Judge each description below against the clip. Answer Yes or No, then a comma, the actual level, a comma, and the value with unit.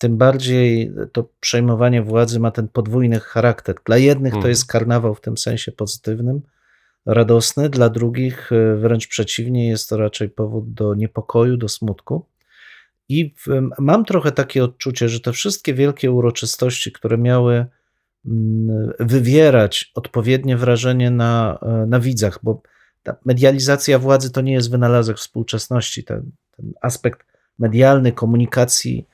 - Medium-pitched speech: No, low, 120 Hz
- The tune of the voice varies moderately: No, narrow, 2.3 semitones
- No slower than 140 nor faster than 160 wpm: No, average, 130 wpm